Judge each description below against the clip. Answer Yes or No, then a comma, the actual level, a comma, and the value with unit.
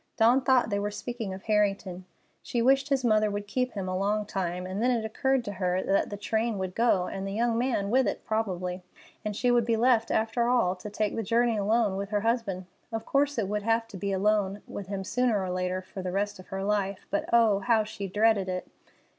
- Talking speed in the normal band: No, fast, 235 wpm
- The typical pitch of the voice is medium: No, high, 210 Hz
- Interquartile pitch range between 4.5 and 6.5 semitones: No, average, 3.2 semitones